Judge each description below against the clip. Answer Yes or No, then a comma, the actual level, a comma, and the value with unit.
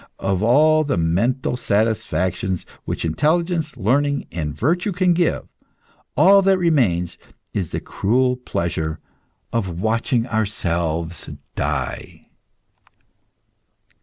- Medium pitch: No, low, 115 Hz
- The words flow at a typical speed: No, slow, 100 wpm